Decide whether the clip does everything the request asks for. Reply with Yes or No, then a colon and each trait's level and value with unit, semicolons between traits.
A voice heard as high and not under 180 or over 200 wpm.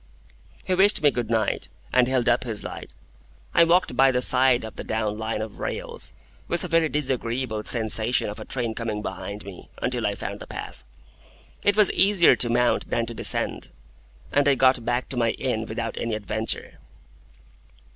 No: low, 120 Hz; average, 185 wpm